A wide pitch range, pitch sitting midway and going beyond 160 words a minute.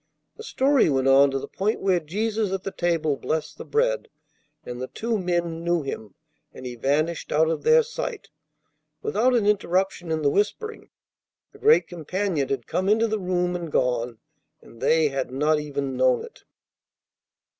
Yes: wide, 6.9 semitones; medium, 170 Hz; average, 175 wpm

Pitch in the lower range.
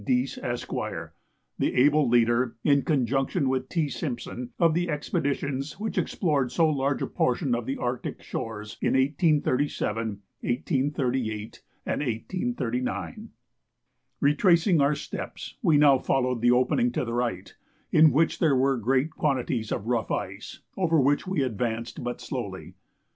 Yes: low, 130 Hz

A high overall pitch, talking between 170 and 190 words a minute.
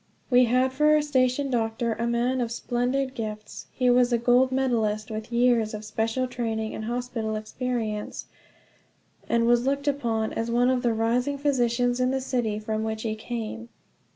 Yes: high, 240 Hz; average, 175 wpm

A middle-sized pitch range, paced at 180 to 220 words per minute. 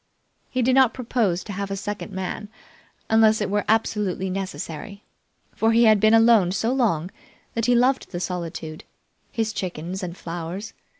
No: average, 3.7 semitones; average, 165 wpm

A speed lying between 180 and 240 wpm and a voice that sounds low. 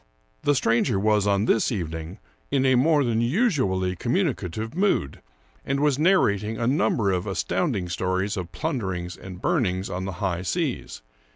No: average, 160 wpm; low, 110 Hz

